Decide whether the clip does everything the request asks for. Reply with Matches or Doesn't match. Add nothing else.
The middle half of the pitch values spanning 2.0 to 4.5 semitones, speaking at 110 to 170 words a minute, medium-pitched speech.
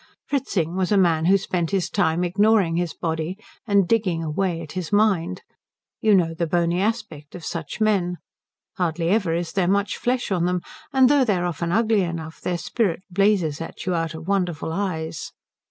Doesn't match